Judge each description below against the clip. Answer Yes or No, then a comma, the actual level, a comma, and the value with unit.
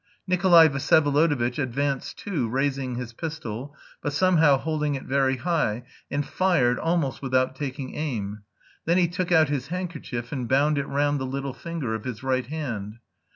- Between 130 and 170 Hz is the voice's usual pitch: Yes, medium, 140 Hz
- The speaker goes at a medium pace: Yes, average, 160 wpm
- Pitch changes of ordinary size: Yes, average, 3.7 semitones